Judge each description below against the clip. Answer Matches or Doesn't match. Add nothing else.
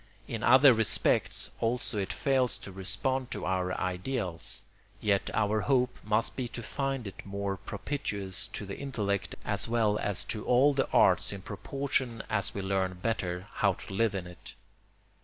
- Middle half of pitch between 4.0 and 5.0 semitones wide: Matches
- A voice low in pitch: Matches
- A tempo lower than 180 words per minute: Matches